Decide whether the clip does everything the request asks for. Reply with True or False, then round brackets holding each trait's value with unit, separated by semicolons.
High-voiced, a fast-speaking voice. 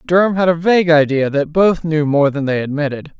False (155 Hz; 225 wpm)